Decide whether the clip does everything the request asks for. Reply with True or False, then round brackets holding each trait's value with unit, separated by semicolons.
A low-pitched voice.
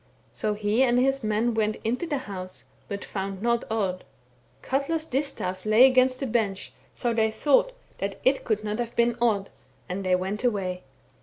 False (220 Hz)